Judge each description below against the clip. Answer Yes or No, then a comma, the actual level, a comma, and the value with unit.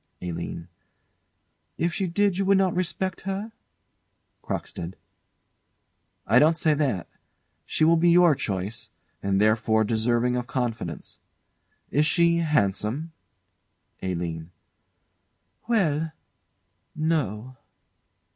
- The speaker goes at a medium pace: No, slow, 100 wpm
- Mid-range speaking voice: Yes, medium, 145 Hz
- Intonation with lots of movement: Yes, wide, 8.1 semitones